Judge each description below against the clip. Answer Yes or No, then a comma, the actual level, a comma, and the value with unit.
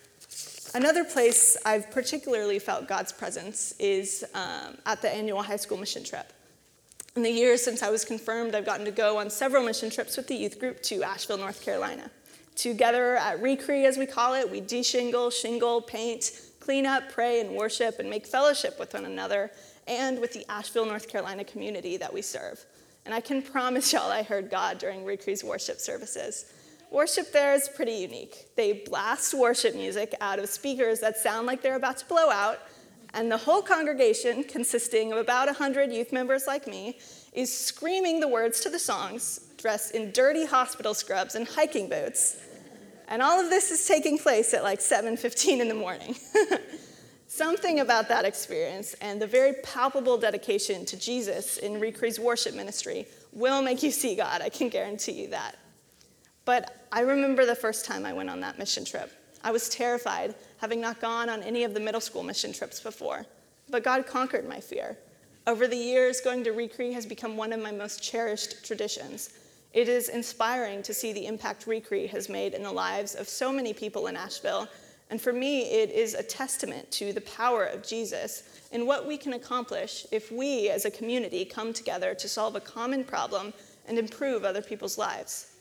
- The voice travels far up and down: No, average, 3.8 semitones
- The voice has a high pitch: Yes, high, 245 Hz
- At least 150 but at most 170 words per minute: No, average, 190 wpm